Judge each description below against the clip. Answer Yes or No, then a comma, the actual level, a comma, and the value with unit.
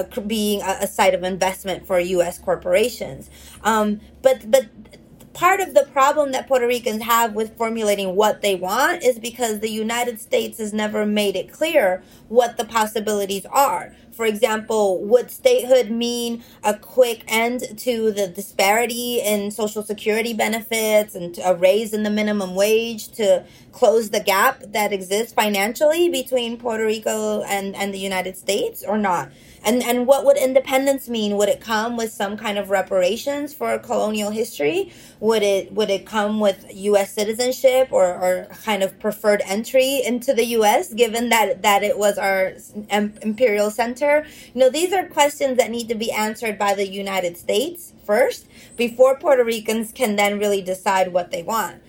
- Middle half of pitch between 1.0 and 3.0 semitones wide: No, average, 3.5 semitones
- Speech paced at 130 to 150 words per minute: No, average, 170 wpm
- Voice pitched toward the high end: Yes, high, 220 Hz